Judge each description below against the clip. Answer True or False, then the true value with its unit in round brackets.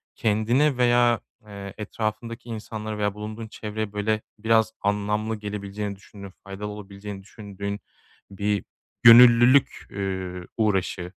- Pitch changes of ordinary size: False (1.8 semitones)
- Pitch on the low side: True (105 Hz)